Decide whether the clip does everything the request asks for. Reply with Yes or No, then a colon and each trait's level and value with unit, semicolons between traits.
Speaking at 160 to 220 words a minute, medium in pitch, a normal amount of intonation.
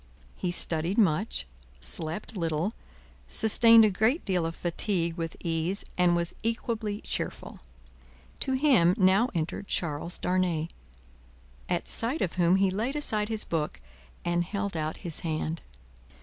No: slow, 135 wpm; medium, 180 Hz; average, 4.5 semitones